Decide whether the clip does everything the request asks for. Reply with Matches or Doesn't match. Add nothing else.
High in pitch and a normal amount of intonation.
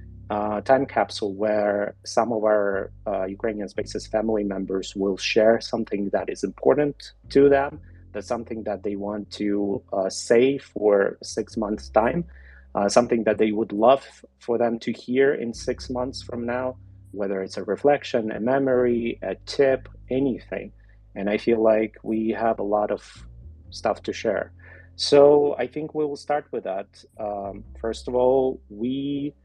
Doesn't match